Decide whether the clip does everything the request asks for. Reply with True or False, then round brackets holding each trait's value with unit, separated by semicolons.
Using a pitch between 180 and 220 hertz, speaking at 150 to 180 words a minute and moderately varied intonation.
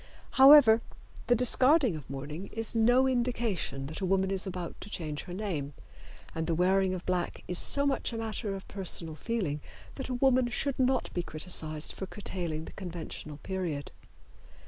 False (190 Hz; 170 wpm; 6.7 semitones)